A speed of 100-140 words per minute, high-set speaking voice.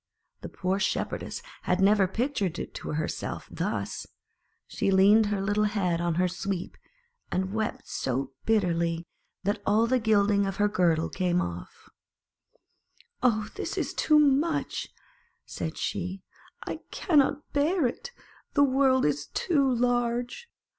Yes: slow, 135 wpm; high, 205 Hz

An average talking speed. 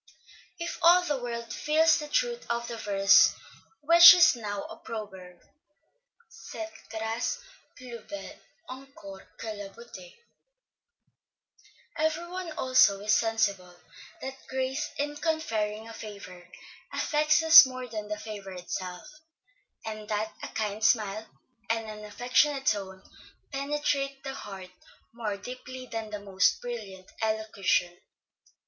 No: slow, 125 wpm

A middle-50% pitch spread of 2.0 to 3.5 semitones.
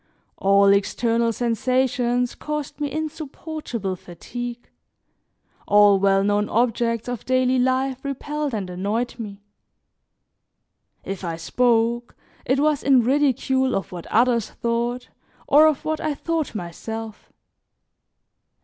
No: average, 4.4 semitones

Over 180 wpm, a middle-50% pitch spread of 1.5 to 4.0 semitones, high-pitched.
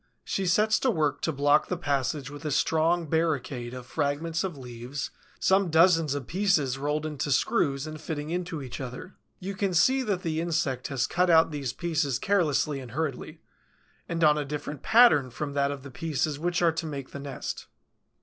No: average, 190 wpm; average, 3.5 semitones; medium, 150 Hz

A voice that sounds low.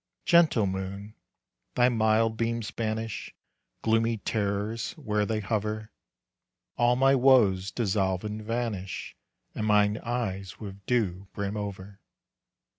Yes: low, 110 Hz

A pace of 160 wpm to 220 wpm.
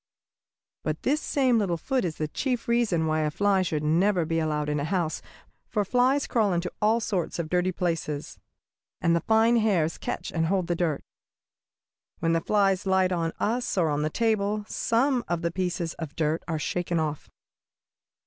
Yes: average, 185 wpm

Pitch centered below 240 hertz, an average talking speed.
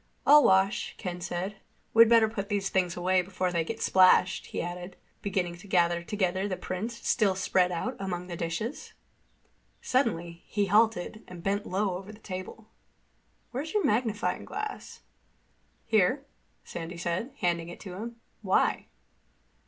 Yes: high, 190 Hz; average, 150 wpm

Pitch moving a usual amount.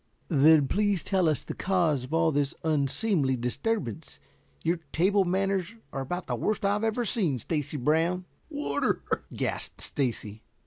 No: wide, 5.7 semitones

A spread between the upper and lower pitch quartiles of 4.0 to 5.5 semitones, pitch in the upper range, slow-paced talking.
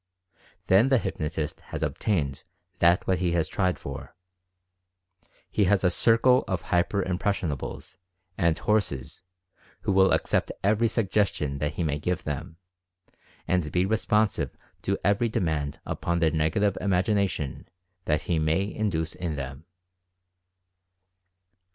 No: average, 4.3 semitones; very low, 90 Hz; slow, 130 wpm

